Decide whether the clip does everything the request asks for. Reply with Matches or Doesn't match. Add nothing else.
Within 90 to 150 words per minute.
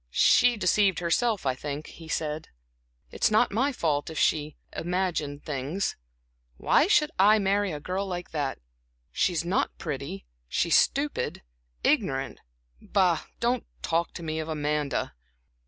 Matches